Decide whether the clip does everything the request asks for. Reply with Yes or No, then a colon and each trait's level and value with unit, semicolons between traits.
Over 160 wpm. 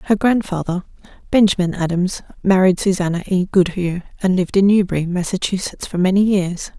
No: average, 140 wpm